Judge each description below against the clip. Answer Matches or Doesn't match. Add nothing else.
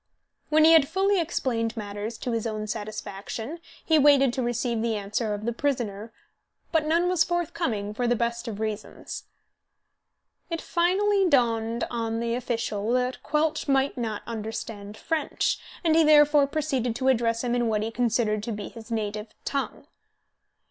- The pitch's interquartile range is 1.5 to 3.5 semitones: Doesn't match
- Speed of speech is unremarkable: Matches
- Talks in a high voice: Matches